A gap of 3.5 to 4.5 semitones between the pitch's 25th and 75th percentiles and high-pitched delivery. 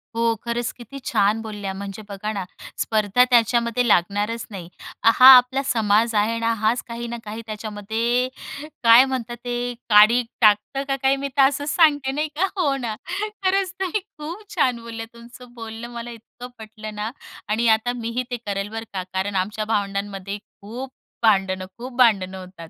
No: average, 3.0 semitones; high, 230 Hz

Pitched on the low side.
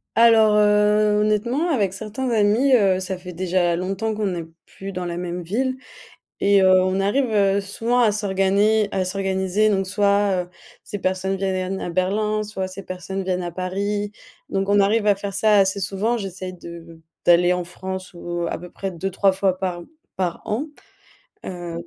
No: high, 195 Hz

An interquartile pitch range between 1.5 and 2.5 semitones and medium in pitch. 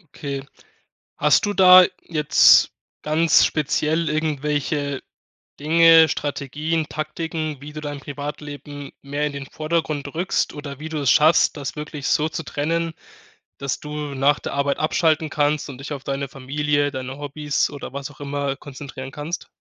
Yes: narrow, 1.8 semitones; medium, 150 Hz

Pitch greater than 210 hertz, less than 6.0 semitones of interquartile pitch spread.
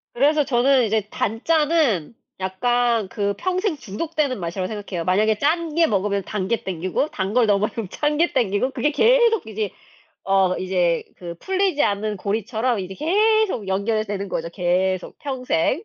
No: high, 220 Hz; wide, 7.4 semitones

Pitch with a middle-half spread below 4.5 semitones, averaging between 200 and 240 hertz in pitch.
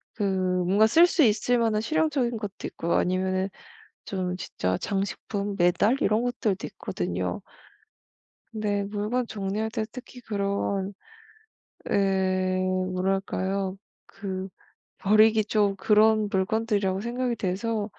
Yes: average, 2.7 semitones; high, 205 Hz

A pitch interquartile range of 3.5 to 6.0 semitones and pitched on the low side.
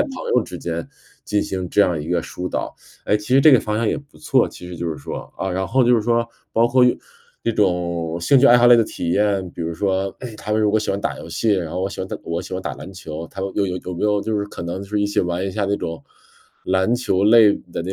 Yes: average, 3.8 semitones; low, 100 Hz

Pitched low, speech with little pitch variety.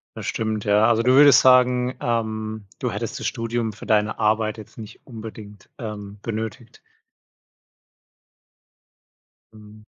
Yes: low, 110 Hz; narrow, 1.5 semitones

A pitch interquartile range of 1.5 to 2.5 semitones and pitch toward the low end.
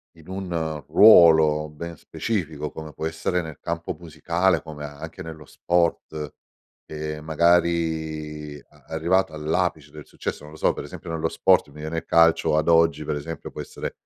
Yes: narrow, 1.8 semitones; very low, 80 Hz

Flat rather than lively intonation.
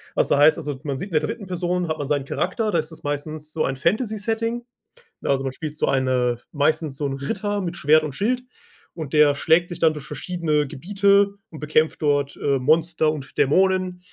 No: average, 4.1 semitones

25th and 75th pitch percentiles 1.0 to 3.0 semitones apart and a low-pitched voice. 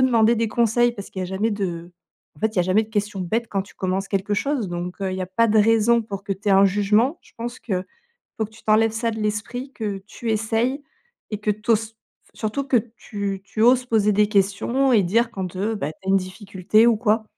No: average, 2.7 semitones; high, 215 Hz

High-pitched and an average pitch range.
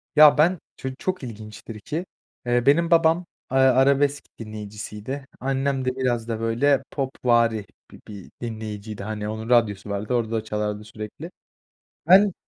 No: low, 120 Hz; average, 4.5 semitones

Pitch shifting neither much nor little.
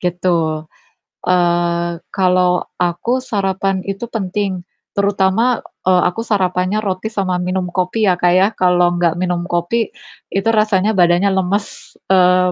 No: narrow, 2.0 semitones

